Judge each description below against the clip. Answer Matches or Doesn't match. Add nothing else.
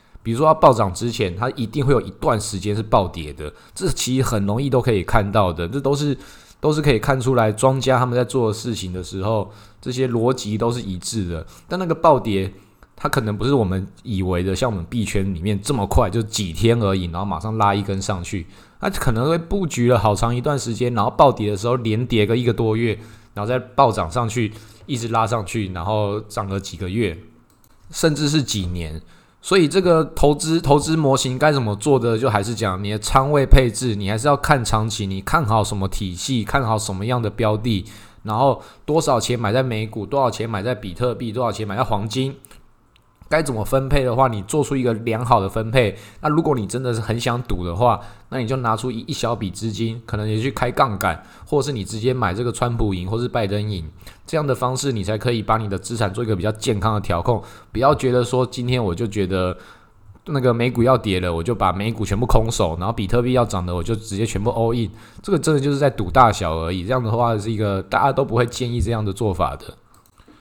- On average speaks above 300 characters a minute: Matches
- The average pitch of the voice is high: Doesn't match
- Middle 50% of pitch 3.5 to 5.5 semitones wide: Matches